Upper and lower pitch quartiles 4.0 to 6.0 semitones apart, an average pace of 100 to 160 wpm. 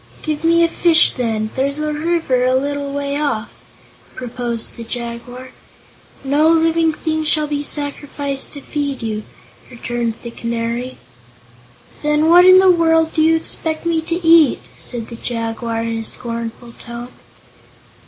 Yes: average, 5.1 semitones; average, 150 wpm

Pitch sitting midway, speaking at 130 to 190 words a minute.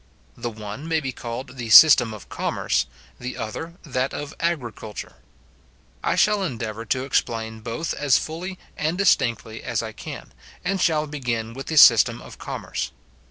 No: low, 130 Hz; average, 160 wpm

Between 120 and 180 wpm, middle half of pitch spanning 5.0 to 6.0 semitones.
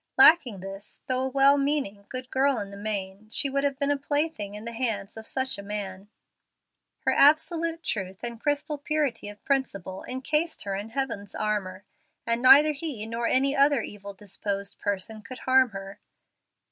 Yes: average, 175 wpm; wide, 5.5 semitones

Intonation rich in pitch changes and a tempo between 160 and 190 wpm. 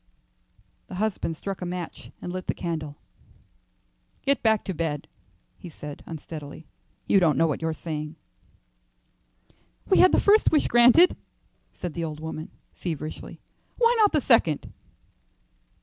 No: wide, 5.9 semitones; average, 145 wpm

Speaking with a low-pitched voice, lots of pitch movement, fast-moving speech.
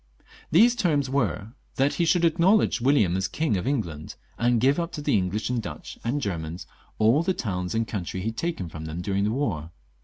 Yes: low, 115 Hz; wide, 7.9 semitones; fast, 210 wpm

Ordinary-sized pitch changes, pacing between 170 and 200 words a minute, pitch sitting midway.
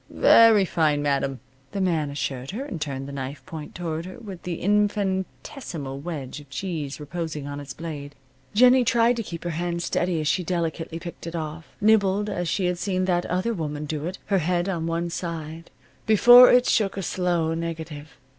Yes: average, 3.9 semitones; average, 190 wpm; medium, 170 Hz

